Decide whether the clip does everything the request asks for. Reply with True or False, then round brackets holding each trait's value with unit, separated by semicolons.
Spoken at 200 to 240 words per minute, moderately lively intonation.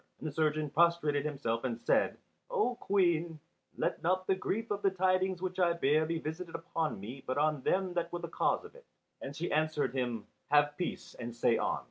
True (205 wpm; 4.1 semitones)